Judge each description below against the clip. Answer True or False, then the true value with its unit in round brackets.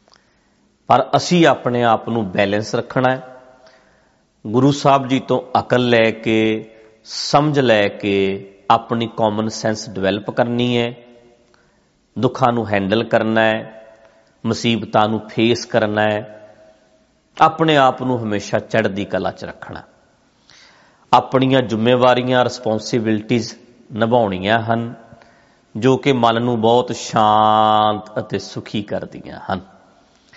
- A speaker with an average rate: False (115 wpm)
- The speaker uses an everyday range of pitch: False (2.3 semitones)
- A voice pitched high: False (115 Hz)